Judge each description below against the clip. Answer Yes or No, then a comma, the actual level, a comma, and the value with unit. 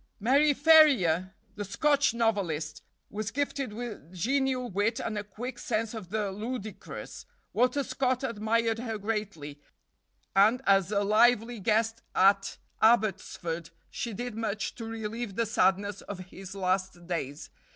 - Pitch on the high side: Yes, high, 215 Hz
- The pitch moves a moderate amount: Yes, average, 3.7 semitones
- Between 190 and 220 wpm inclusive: No, slow, 135 wpm